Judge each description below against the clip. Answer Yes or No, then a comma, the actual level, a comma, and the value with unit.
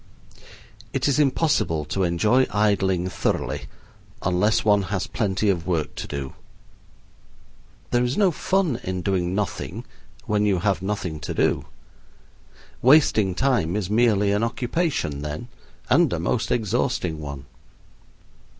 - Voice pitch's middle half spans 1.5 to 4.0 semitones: No, average, 5.1 semitones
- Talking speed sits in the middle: No, slow, 130 wpm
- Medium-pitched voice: No, low, 100 Hz